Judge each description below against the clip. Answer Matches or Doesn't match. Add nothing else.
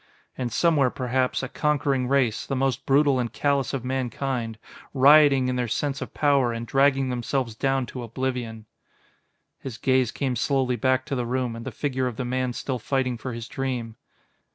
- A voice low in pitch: Matches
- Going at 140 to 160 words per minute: Doesn't match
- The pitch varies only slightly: Matches